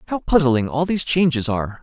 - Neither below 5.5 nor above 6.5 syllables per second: Yes, 6.3 syllables/s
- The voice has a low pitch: No, medium, 145 Hz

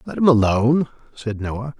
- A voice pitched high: No, low, 120 Hz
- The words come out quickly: No, average, 165 wpm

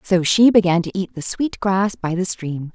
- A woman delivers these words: Yes, female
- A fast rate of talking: Yes, fast, 240 wpm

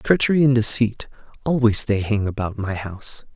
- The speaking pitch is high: No, low, 115 Hz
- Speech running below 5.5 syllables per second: Yes, 5.2 syllables/s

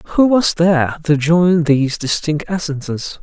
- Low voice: No, medium, 160 Hz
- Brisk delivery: No, average, 150 wpm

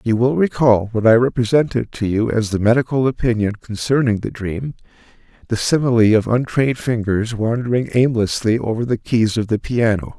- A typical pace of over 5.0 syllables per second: Yes, 5.3 syllables/s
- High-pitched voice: No, low, 115 Hz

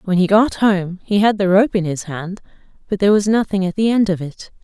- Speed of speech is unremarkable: No, fast, 260 wpm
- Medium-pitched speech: No, high, 195 Hz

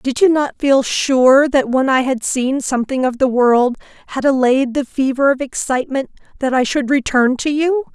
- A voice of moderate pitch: No, very high, 265 Hz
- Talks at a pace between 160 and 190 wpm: Yes, average, 180 wpm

